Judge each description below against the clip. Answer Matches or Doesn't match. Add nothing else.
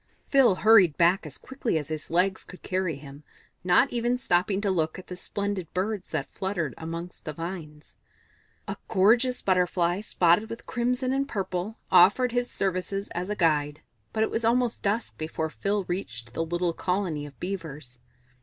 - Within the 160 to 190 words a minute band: Matches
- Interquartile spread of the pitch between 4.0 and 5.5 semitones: Matches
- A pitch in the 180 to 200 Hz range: Matches